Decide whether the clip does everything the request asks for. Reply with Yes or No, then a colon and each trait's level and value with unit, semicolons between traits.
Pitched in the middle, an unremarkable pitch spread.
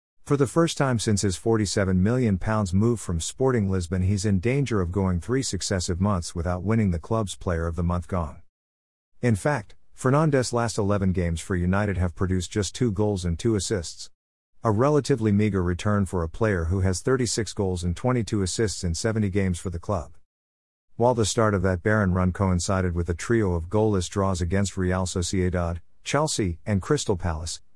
No: very low, 95 Hz; average, 3.9 semitones